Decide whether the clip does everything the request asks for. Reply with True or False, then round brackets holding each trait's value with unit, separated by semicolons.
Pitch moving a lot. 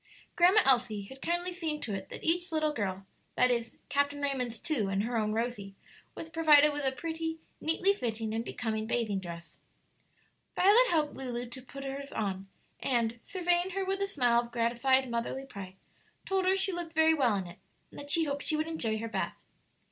True (6.2 semitones)